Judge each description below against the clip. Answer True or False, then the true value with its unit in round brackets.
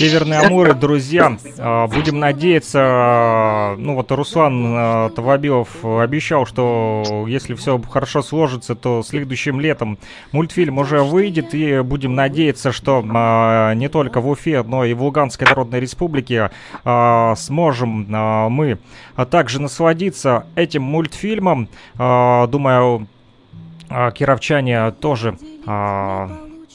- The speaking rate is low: True (100 wpm)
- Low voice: True (130 Hz)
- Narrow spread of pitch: False (4.4 semitones)